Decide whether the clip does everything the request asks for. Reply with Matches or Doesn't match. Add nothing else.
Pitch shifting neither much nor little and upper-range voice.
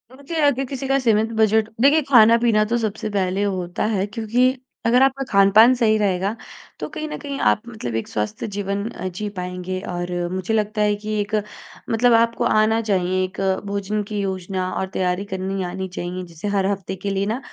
Matches